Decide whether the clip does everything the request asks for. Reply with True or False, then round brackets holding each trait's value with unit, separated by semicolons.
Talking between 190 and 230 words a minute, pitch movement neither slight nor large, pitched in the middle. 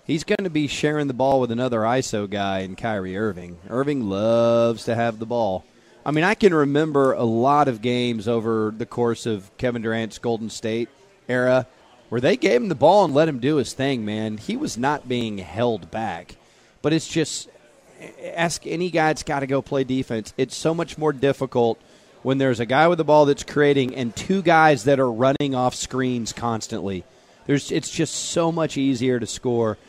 False (200 wpm; 4.3 semitones; 130 Hz)